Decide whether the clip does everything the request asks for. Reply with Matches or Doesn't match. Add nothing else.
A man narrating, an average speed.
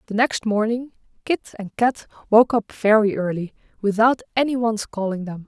Doesn't match